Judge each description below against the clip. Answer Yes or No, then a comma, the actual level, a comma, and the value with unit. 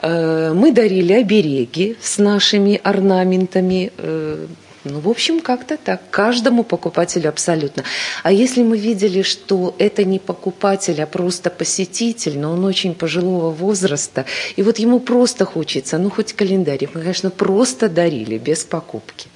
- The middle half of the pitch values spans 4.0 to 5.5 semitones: Yes, average, 4.3 semitones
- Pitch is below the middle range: No, medium, 185 Hz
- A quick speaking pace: No, average, 135 wpm